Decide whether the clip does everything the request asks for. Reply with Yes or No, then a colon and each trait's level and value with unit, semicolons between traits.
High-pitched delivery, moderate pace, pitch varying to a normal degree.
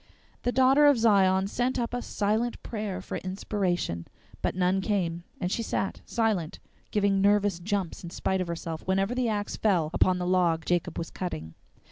Yes: high, 195 Hz; average, 175 wpm; average, 3.4 semitones